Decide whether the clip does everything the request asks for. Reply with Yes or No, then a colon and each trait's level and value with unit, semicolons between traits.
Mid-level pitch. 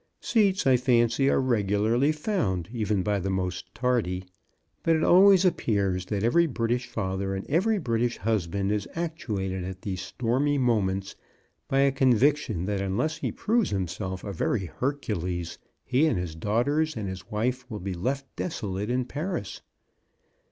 No: low, 115 Hz